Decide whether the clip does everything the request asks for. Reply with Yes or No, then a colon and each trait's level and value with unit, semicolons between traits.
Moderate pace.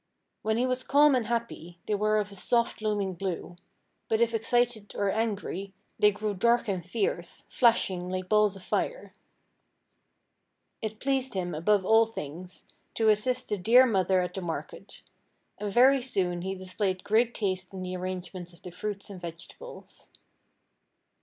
Yes: average, 160 wpm